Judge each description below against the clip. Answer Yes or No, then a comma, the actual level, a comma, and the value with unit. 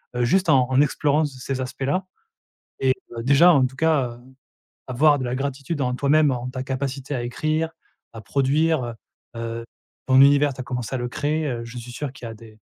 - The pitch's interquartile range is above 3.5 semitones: No, average, 2.8 semitones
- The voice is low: Yes, low, 130 Hz